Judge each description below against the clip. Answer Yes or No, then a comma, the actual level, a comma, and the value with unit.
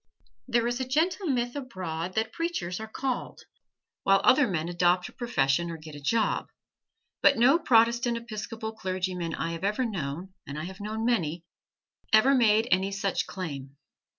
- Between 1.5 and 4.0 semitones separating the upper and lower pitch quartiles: No, wide, 5.6 semitones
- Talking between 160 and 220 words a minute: Yes, average, 165 wpm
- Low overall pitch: No, high, 210 Hz